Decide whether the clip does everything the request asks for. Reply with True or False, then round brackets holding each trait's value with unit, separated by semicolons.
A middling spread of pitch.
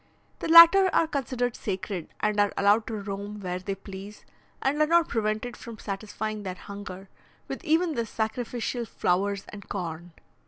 True (3.9 semitones)